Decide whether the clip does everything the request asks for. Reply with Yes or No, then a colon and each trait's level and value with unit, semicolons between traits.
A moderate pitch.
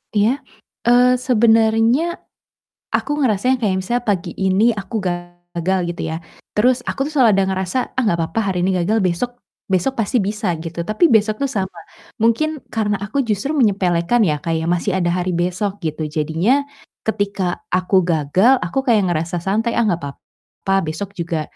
No: high, 200 Hz